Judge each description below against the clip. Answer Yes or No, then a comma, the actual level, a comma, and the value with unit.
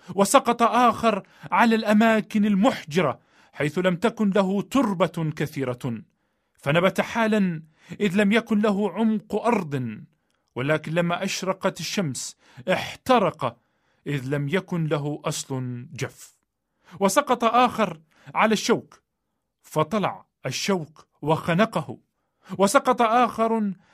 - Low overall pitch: No, high, 190 Hz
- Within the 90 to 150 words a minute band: Yes, average, 100 wpm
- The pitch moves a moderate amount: No, wide, 5.8 semitones